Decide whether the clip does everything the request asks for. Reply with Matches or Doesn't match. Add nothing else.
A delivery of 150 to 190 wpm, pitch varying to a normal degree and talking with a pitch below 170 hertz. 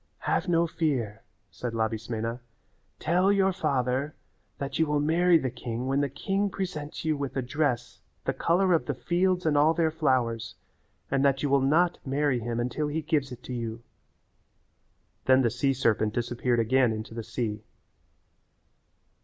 Matches